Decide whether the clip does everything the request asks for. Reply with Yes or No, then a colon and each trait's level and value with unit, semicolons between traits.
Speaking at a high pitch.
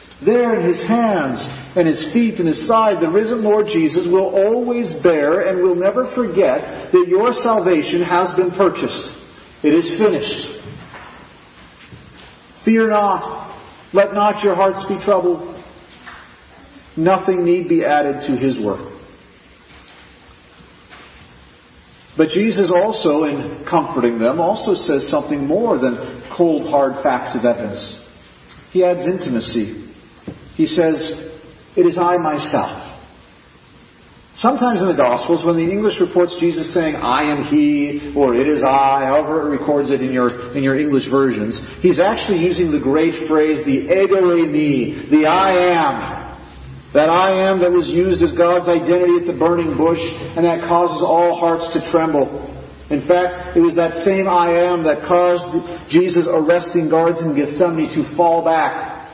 No: medium, 170 Hz